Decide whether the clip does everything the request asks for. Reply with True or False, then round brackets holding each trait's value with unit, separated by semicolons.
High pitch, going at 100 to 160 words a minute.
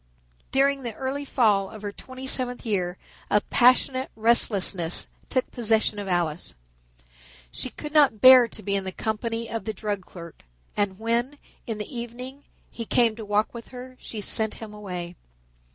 False (225 Hz; 170 wpm)